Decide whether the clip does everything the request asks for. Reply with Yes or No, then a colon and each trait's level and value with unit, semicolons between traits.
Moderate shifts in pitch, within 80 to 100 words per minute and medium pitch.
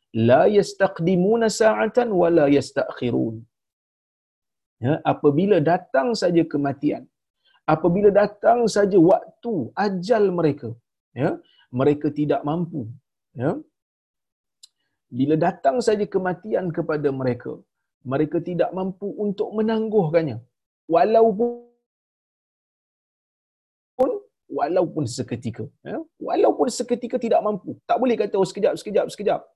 No: wide, 7.2 semitones; average, 95 wpm; medium, 180 Hz